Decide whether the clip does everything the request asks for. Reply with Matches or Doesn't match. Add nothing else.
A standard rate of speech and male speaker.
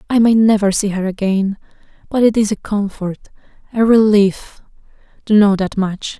Doesn't match